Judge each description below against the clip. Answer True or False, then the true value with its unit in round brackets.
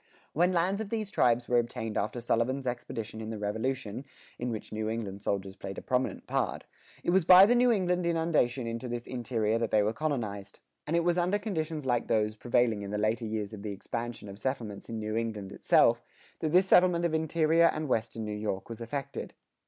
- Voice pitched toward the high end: False (120 Hz)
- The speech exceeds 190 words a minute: True (205 wpm)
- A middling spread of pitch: False (6.8 semitones)